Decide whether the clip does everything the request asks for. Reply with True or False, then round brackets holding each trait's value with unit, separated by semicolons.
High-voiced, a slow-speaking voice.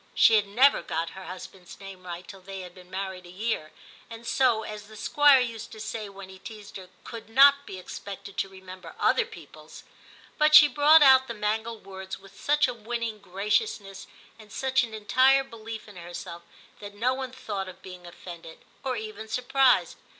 False (210 Hz; 195 wpm)